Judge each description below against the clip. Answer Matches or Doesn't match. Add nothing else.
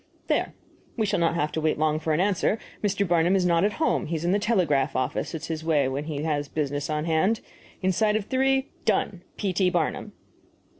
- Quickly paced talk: Matches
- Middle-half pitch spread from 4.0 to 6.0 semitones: Matches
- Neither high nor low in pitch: Matches